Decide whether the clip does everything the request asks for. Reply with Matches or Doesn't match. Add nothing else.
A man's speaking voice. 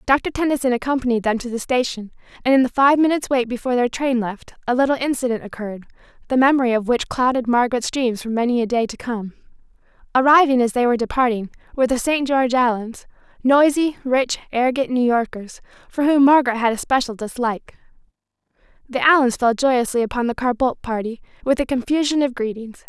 Doesn't match